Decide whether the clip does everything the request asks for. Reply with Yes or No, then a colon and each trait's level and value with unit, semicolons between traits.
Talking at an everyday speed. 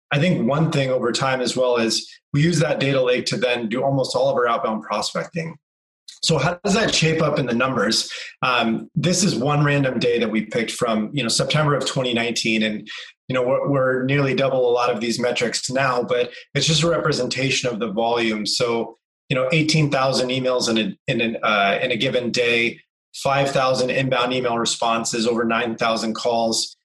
No: fast, 210 wpm